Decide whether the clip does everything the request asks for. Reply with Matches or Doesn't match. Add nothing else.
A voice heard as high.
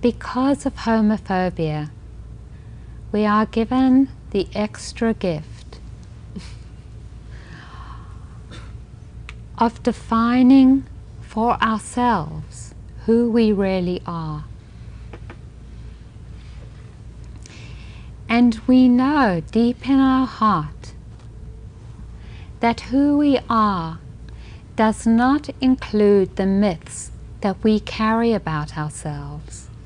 Matches